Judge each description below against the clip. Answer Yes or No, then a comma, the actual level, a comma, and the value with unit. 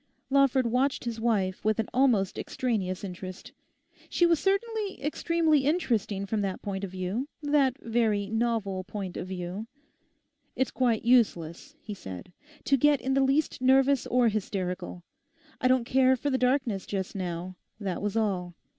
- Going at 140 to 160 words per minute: Yes, average, 155 wpm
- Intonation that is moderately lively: No, wide, 5.7 semitones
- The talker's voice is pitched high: Yes, high, 230 Hz